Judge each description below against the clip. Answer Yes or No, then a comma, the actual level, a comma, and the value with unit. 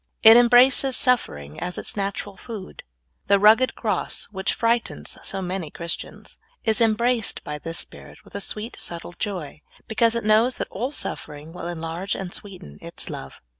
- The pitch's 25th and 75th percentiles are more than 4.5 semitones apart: Yes, average, 5.0 semitones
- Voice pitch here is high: Yes, high, 200 Hz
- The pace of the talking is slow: No, average, 170 wpm